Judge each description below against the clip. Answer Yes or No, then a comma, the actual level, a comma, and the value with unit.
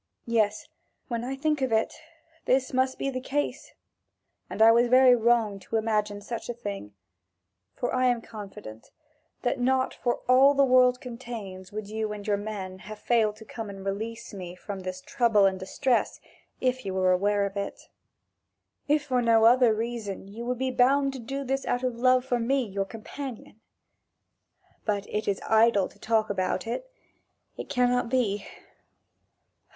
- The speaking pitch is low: No, high, 230 Hz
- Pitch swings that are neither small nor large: Yes, average, 3.7 semitones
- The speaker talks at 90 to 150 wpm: No, average, 170 wpm